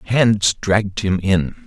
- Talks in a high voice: No, low, 100 Hz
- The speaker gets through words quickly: No, average, 145 wpm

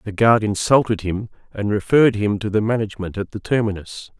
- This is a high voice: No, low, 105 Hz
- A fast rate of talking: No, average, 185 wpm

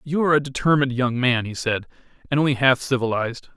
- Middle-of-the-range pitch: No, low, 130 Hz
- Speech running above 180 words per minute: Yes, average, 200 wpm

